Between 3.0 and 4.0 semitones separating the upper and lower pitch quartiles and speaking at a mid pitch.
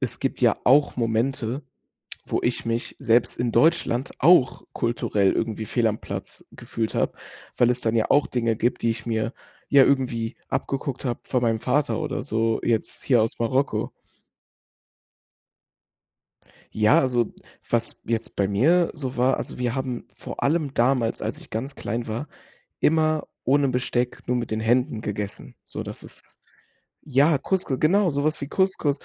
No: average, 3.6 semitones; low, 125 Hz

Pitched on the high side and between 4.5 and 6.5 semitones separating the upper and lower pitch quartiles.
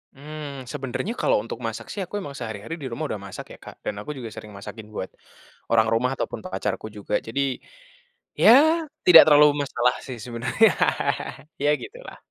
No: low, 125 Hz; average, 4.8 semitones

